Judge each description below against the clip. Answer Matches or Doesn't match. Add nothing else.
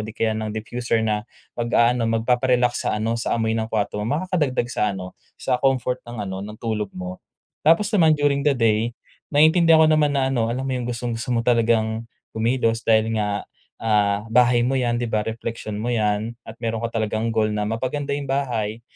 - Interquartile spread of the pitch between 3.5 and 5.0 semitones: Doesn't match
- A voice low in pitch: Matches